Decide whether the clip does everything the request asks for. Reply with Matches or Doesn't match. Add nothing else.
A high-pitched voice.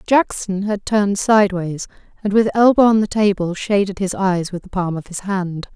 Matches